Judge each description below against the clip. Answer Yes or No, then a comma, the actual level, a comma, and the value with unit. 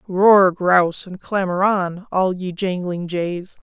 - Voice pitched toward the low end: No, medium, 185 Hz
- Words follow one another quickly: No, average, 145 wpm